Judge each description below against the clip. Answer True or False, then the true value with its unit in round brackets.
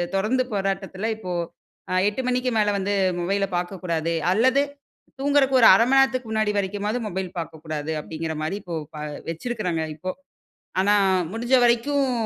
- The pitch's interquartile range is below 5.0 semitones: False (5.3 semitones)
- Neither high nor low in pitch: False (200 Hz)